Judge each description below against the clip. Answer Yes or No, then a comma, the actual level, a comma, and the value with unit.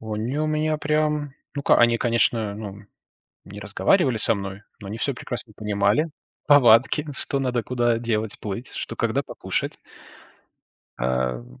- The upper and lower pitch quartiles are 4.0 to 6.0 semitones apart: Yes, average, 5.1 semitones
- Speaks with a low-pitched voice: Yes, low, 115 Hz